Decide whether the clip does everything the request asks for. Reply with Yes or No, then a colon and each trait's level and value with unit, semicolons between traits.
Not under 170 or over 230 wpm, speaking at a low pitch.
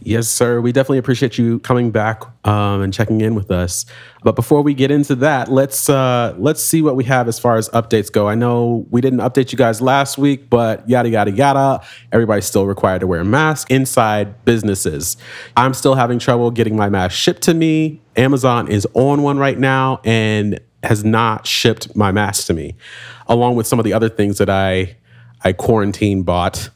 Yes: average, 200 wpm; low, 120 Hz